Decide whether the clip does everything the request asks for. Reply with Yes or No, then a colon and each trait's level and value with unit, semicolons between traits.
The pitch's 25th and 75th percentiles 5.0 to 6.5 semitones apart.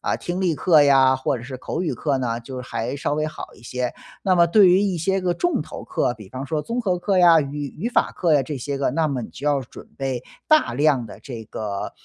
Yes: wide, 5.4 semitones